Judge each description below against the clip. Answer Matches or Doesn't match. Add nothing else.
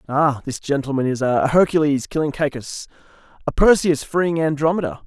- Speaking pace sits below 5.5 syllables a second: Matches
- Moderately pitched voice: Matches